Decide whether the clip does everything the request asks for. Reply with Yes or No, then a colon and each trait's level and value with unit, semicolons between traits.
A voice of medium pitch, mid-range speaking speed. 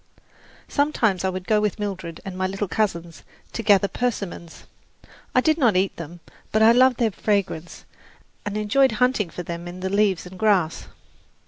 No: high, 200 Hz; average, 175 wpm